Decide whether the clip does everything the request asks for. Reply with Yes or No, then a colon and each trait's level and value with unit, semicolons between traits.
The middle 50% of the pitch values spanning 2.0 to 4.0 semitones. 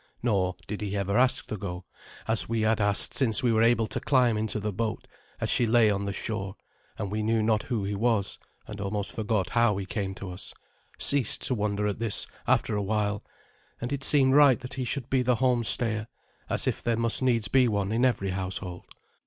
Yes: average, 3.0 semitones